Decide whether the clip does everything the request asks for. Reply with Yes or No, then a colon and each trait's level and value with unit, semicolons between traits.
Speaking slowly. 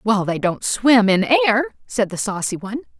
No: average, 200 wpm